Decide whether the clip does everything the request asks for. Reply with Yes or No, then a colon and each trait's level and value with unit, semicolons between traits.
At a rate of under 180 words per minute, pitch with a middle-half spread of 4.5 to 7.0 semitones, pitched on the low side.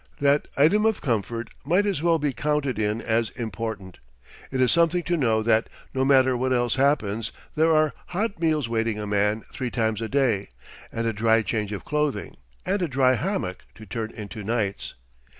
No: average, 185 wpm; average, 5.3 semitones; low, 120 Hz